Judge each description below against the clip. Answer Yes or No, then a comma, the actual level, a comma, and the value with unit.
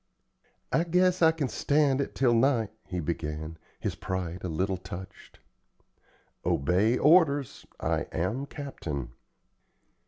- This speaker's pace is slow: Yes, slow, 120 wpm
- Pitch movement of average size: No, wide, 8.5 semitones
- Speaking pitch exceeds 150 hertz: No, low, 110 Hz